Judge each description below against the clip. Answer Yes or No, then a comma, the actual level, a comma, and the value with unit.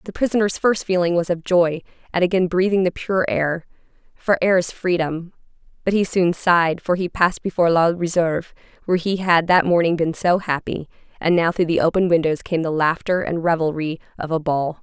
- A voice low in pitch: No, medium, 175 Hz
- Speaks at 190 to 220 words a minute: Yes, average, 195 wpm